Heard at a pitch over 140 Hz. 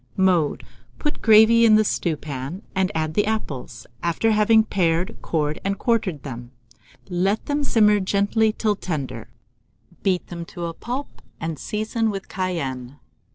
Yes: high, 190 Hz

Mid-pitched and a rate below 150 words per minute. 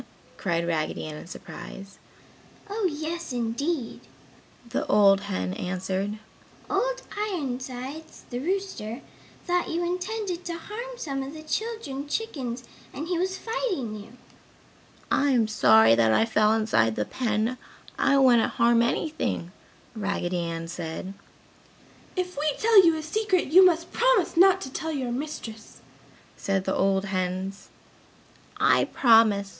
No: very high, 255 Hz; slow, 135 wpm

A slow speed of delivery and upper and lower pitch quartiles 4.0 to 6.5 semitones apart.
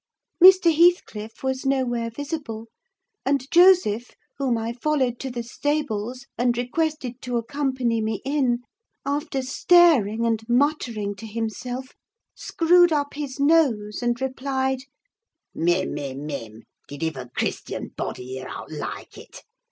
Yes: slow, 125 wpm; average, 4.4 semitones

